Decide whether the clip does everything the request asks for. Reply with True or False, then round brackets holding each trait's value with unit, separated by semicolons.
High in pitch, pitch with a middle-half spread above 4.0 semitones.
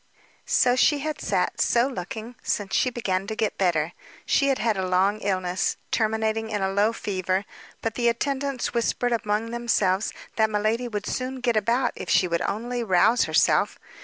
False (220 Hz; 3.5 semitones)